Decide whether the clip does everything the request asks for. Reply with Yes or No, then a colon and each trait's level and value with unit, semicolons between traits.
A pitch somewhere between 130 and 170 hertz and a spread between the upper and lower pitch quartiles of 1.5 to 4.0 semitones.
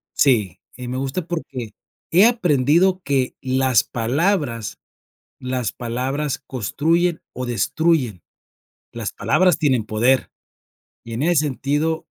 No: low, 135 Hz; average, 4.7 semitones